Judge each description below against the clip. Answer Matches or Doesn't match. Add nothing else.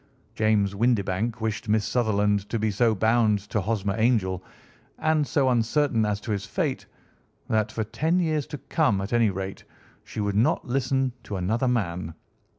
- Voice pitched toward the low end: Matches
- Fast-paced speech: Doesn't match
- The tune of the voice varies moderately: Matches